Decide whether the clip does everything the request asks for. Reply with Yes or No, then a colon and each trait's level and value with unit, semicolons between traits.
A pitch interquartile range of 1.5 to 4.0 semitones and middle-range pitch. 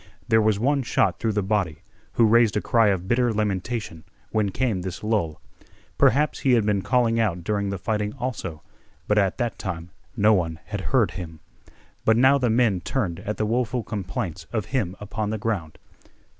No: average, 3.7 semitones; low, 105 Hz